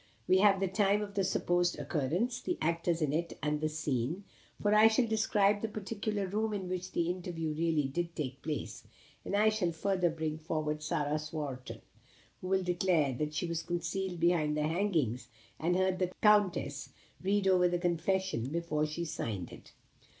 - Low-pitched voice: No, medium, 175 Hz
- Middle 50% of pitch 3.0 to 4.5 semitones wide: Yes, average, 4.0 semitones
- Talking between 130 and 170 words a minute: No, average, 180 wpm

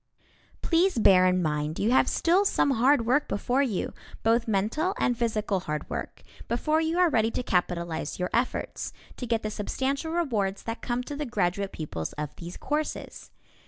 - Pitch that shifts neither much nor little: No, wide, 7.3 semitones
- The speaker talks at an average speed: Yes, average, 175 wpm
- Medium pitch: No, high, 230 Hz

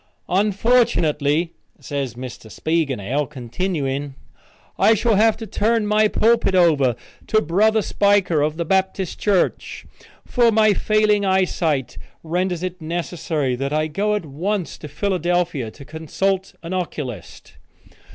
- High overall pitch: No, medium, 175 Hz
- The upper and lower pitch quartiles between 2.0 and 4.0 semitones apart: No, wide, 5.5 semitones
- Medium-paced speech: No, slow, 125 wpm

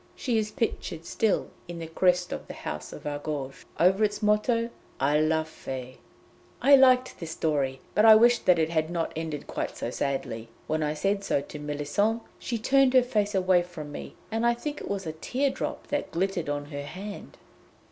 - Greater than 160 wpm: Yes, average, 200 wpm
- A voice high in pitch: No, medium, 180 Hz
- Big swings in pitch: Yes, wide, 6.7 semitones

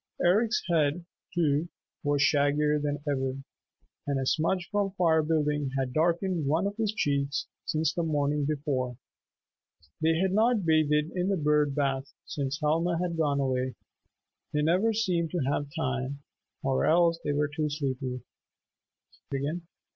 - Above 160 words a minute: No, average, 140 wpm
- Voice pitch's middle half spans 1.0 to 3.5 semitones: Yes, average, 3.2 semitones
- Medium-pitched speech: Yes, medium, 150 Hz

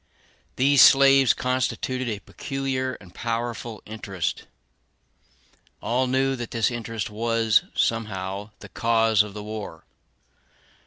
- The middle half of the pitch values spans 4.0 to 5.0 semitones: No, average, 3.4 semitones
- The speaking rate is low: Yes, slow, 110 wpm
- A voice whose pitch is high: No, low, 115 Hz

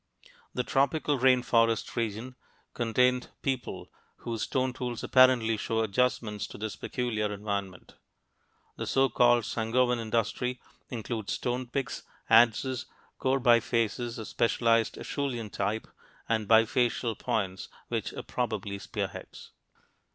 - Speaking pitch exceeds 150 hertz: No, low, 115 Hz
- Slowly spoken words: Yes, slow, 115 wpm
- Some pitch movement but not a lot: No, narrow, 2.3 semitones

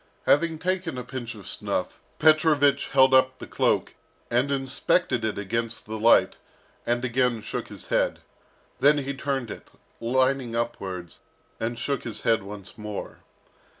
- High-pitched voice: No, low, 125 Hz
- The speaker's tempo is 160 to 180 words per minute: No, average, 150 wpm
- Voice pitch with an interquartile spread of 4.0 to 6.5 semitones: No, average, 3.4 semitones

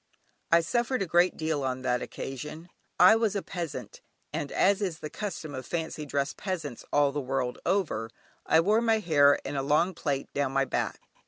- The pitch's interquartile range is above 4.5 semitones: Yes, average, 5.2 semitones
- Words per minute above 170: Yes, average, 190 wpm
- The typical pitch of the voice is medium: Yes, medium, 155 Hz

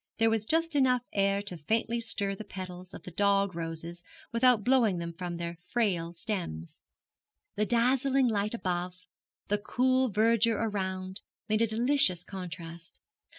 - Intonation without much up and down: No, average, 4.5 semitones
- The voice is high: Yes, high, 205 Hz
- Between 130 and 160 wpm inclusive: Yes, average, 150 wpm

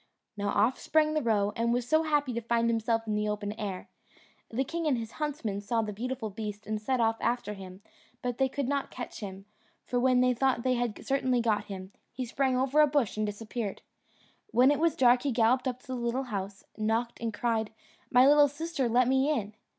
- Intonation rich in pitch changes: No, average, 3.7 semitones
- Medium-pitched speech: No, high, 240 Hz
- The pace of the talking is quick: Yes, fast, 220 wpm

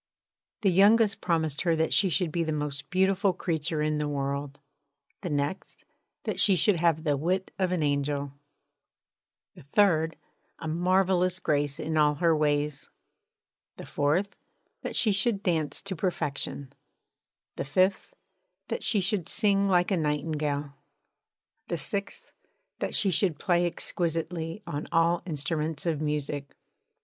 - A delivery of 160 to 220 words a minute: No, average, 140 wpm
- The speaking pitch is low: No, medium, 165 Hz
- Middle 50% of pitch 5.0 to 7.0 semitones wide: No, average, 4.1 semitones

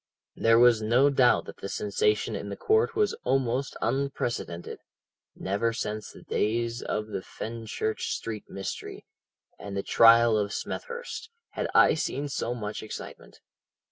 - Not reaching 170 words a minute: Yes, average, 140 wpm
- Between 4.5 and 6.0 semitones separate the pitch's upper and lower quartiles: No, average, 4.0 semitones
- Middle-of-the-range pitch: No, low, 115 Hz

